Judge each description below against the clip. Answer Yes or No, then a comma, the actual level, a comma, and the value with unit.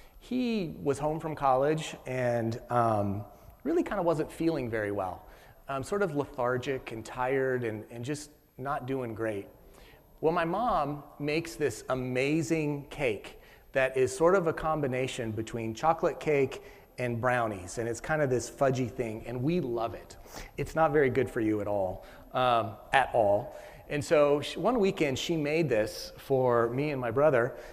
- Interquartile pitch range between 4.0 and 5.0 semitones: Yes, average, 4.6 semitones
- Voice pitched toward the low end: Yes, low, 130 Hz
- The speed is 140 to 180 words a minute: Yes, average, 170 wpm